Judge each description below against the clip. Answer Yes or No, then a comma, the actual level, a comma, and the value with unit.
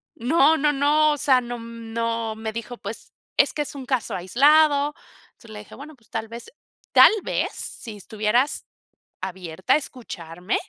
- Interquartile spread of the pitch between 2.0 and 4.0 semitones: No, average, 4.5 semitones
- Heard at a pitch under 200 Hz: No, high, 230 Hz